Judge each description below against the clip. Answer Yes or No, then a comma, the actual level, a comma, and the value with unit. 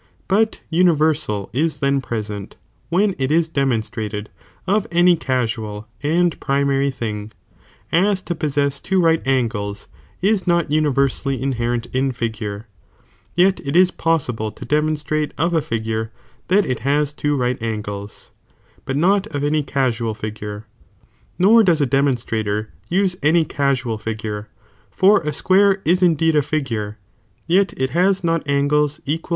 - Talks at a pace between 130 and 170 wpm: Yes, average, 150 wpm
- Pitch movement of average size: No, wide, 6.5 semitones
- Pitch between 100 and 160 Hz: Yes, medium, 140 Hz